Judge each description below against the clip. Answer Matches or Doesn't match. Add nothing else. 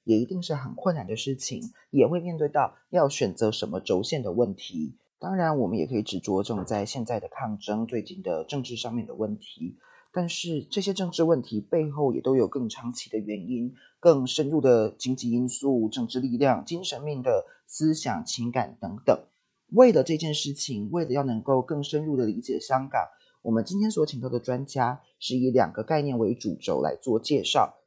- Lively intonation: Doesn't match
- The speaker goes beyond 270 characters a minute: Matches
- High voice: Doesn't match